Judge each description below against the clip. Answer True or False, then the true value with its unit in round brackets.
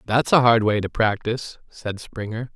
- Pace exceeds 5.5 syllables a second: False (4.8 syllables/s)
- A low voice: True (115 Hz)